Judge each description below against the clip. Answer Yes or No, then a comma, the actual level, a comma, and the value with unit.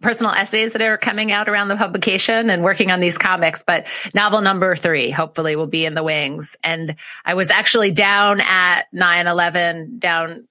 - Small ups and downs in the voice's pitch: No, average, 4.3 semitones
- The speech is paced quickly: No, average, 190 wpm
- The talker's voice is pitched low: No, medium, 185 Hz